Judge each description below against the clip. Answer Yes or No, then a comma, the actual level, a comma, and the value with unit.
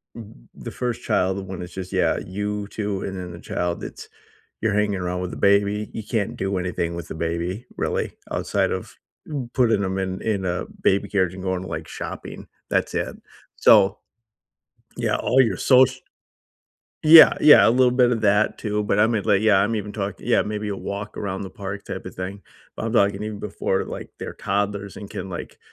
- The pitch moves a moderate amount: No, narrow, 2.2 semitones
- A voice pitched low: Yes, low, 100 Hz